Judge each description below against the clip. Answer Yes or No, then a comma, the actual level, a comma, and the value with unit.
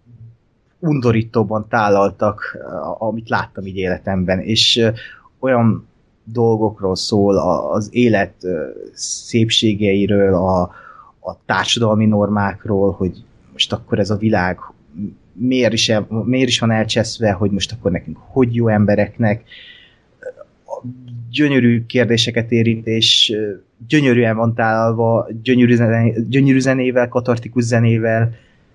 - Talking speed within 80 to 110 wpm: Yes, slow, 105 wpm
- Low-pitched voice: Yes, low, 115 Hz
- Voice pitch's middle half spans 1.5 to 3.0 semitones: Yes, narrow, 2.5 semitones